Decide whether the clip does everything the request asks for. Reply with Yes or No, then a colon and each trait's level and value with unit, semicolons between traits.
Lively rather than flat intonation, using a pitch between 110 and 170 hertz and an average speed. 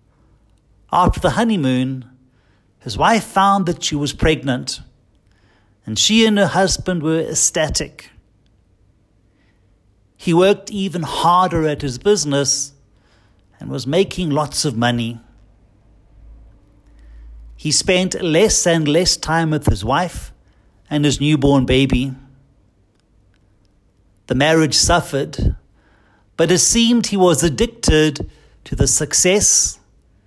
No: wide, 8.4 semitones; low, 135 Hz; slow, 110 wpm